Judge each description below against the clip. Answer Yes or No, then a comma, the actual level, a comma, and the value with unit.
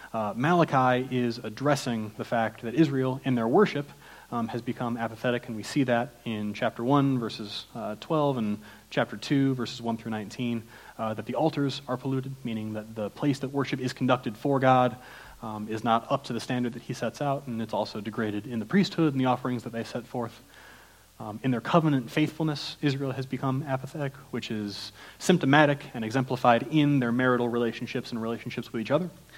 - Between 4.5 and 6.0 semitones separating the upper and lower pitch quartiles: No, average, 3.3 semitones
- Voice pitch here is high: No, low, 125 Hz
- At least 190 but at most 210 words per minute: Yes, average, 195 wpm